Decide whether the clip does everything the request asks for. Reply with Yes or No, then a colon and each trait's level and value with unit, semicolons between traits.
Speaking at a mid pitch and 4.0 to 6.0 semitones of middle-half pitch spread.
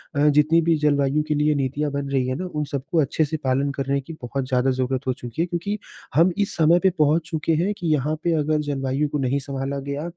No: medium, 145 Hz; average, 2.9 semitones